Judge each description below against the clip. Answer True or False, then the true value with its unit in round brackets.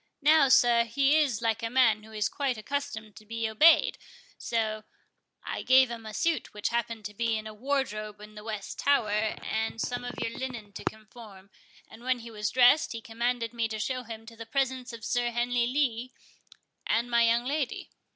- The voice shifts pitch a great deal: False (2.6 semitones)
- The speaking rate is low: False (200 wpm)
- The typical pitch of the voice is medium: False (230 Hz)